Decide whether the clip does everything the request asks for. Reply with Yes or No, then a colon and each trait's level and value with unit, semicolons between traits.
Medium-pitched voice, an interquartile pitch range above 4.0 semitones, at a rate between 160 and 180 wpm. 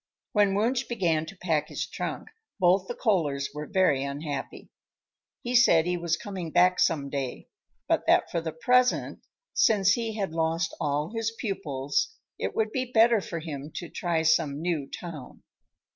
Yes: medium, 170 Hz; wide, 5.4 semitones; average, 165 wpm